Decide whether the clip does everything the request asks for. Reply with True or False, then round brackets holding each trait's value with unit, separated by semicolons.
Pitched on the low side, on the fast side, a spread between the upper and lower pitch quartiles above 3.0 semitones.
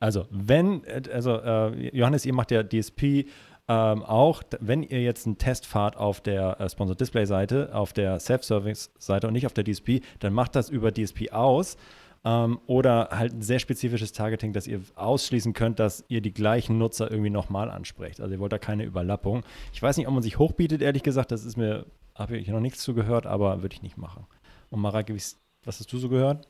True (110 Hz; 200 wpm; 3.5 semitones)